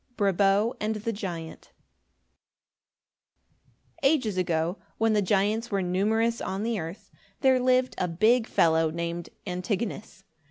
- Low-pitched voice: No, high, 205 Hz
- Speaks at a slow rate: Yes, slow, 120 wpm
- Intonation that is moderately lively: Yes, average, 4.0 semitones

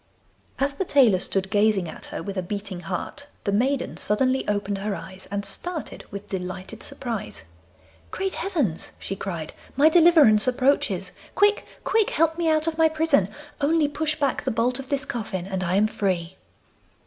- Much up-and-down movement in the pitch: Yes, wide, 7.4 semitones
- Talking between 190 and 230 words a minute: No, average, 170 wpm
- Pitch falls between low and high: No, high, 230 Hz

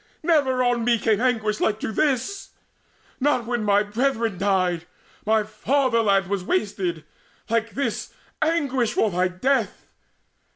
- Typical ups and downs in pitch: Yes, average, 4.2 semitones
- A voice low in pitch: No, high, 225 Hz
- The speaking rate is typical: No, slow, 130 wpm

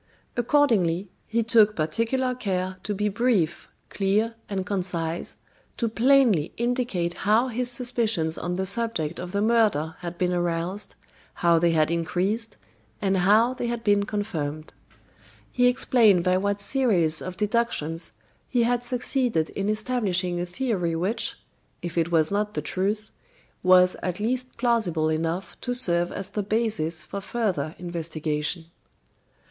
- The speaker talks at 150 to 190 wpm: No, average, 140 wpm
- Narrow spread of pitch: No, average, 5.2 semitones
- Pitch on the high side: Yes, high, 200 Hz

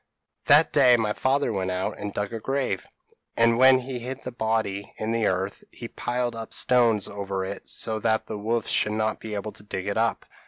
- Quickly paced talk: Yes, fast, 220 wpm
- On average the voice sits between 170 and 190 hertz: No, low, 110 Hz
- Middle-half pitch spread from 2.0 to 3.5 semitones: Yes, average, 3.1 semitones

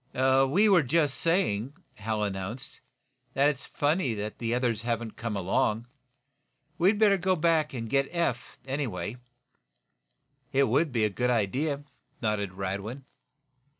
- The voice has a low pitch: Yes, low, 125 Hz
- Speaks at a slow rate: Yes, slow, 130 wpm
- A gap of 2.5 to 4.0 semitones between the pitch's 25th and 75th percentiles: No, wide, 5.6 semitones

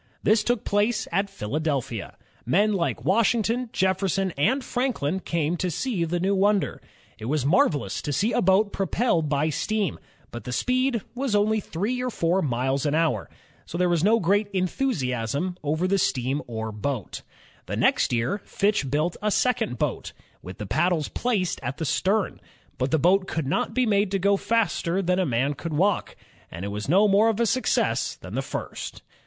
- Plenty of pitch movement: Yes, wide, 6.4 semitones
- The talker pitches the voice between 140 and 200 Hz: Yes, medium, 185 Hz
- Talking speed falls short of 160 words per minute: No, average, 185 wpm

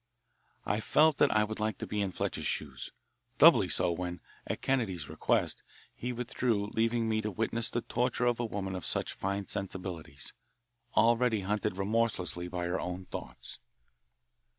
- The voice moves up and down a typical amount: Yes, average, 3.7 semitones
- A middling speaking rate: Yes, average, 160 wpm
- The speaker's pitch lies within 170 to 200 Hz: No, low, 105 Hz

